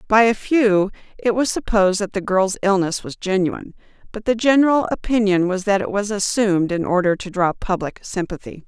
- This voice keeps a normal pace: Yes, average, 185 wpm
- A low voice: No, high, 200 Hz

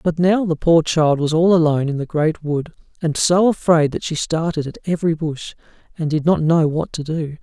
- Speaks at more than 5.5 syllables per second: No, 5.2 syllables/s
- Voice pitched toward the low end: No, medium, 160 Hz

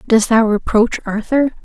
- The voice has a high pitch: Yes, high, 230 Hz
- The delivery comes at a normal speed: Yes, average, 145 wpm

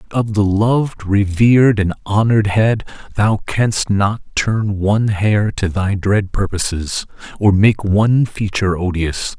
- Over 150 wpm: No, average, 145 wpm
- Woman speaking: No, male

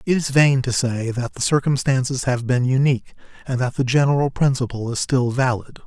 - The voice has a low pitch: Yes, low, 130 Hz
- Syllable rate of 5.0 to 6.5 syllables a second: Yes, 5.5 syllables/s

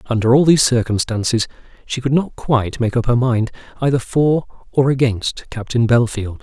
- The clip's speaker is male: Yes, male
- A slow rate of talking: No, average, 170 wpm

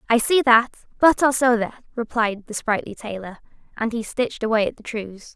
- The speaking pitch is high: Yes, high, 230 Hz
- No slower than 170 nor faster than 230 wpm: Yes, average, 200 wpm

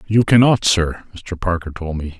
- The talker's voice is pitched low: Yes, very low, 90 Hz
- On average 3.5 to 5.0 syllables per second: Yes, 4.7 syllables/s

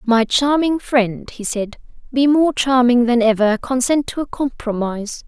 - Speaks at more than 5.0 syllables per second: No, 4.4 syllables/s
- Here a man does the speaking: No, female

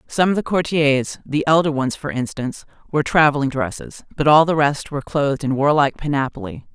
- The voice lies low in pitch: No, medium, 145 Hz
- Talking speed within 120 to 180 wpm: Yes, average, 170 wpm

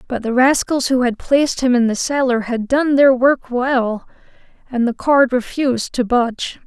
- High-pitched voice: Yes, very high, 250 Hz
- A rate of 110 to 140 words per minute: No, average, 190 wpm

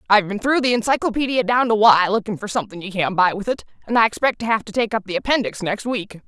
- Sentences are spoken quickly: Yes, fast, 270 wpm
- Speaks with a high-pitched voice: Yes, high, 215 Hz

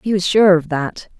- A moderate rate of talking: No, fast, 250 wpm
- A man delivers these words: No, female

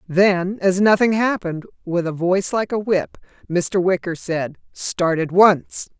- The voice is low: No, medium, 185 Hz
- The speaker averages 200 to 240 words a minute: No, average, 160 wpm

